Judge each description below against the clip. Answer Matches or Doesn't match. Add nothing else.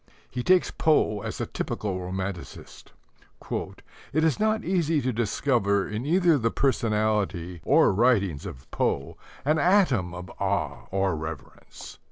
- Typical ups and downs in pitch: Doesn't match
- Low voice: Matches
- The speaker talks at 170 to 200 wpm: Doesn't match